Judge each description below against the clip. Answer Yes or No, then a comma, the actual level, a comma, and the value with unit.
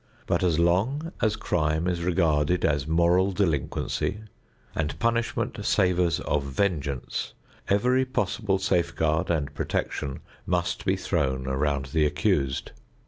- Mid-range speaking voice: No, very low, 85 Hz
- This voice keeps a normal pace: No, slow, 120 wpm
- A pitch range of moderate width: Yes, average, 4.2 semitones